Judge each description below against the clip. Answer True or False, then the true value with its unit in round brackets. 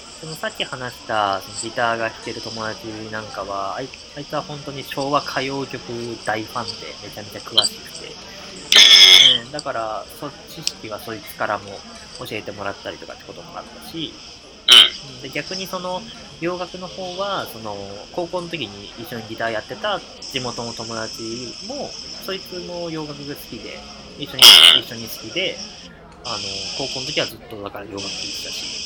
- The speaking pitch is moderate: False (120 Hz)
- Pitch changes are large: True (6.3 semitones)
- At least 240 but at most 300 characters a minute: False (310 characters per minute)